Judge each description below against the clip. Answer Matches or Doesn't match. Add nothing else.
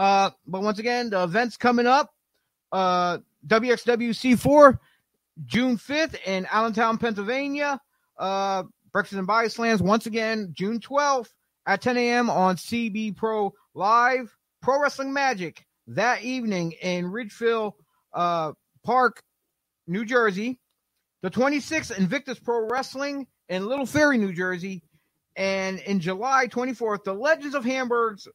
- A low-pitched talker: Doesn't match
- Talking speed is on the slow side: Matches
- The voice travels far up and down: Doesn't match